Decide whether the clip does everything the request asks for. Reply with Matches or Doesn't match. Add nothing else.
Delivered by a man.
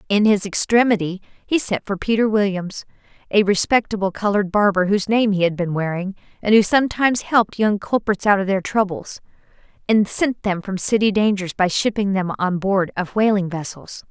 Doesn't match